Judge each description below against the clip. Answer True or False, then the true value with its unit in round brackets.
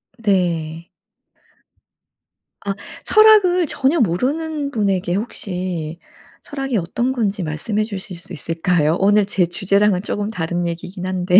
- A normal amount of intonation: True (4.9 semitones)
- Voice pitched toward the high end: True (195 Hz)